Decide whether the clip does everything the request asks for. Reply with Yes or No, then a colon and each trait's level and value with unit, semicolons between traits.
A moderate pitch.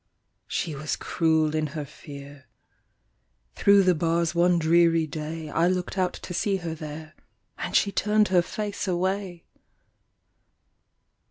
Yes: medium, 170 Hz